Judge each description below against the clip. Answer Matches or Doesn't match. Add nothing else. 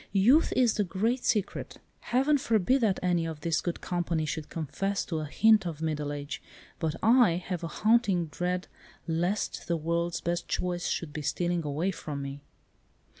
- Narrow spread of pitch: Doesn't match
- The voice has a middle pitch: Matches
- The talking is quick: Doesn't match